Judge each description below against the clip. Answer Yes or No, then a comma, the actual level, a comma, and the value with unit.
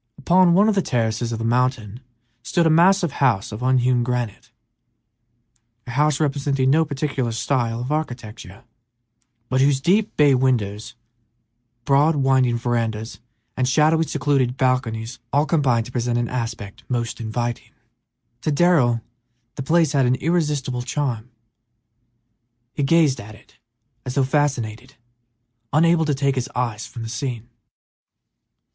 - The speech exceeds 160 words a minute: No, average, 140 wpm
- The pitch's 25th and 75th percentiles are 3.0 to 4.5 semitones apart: Yes, average, 3.8 semitones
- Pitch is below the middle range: Yes, low, 130 Hz